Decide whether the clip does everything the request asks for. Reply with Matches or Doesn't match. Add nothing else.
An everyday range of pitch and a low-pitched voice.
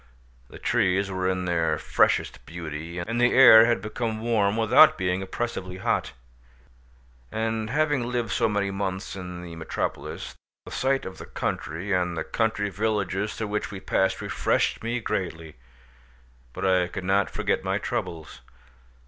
Matches